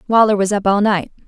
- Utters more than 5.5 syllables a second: Yes, 6.1 syllables/s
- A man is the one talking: No, female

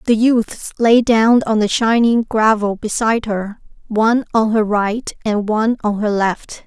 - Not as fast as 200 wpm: Yes, average, 170 wpm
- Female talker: Yes, female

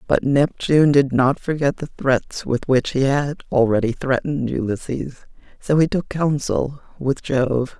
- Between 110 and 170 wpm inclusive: Yes, average, 155 wpm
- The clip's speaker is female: Yes, female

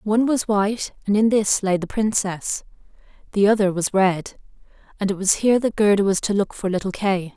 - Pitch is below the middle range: No, high, 200 Hz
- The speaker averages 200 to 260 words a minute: Yes, fast, 205 wpm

